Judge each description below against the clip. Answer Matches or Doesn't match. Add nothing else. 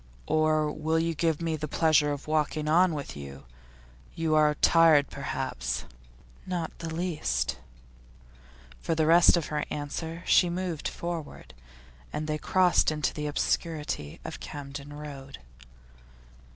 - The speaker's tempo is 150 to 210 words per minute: Doesn't match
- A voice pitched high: Doesn't match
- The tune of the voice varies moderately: Doesn't match